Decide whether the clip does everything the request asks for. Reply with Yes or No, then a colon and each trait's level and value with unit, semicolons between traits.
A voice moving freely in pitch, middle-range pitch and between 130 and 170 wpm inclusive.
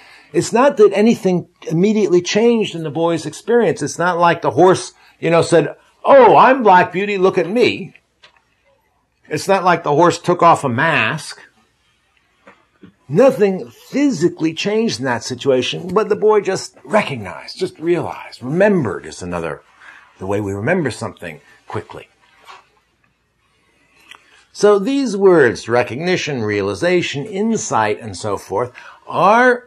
Yes: wide, 5.8 semitones; medium, 180 Hz; slow, 135 wpm